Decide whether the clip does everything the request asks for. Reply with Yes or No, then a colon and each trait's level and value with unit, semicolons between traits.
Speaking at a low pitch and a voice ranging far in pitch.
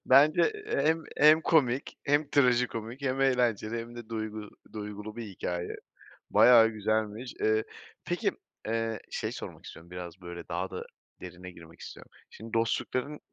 No: low, 115 Hz; average, 3.6 semitones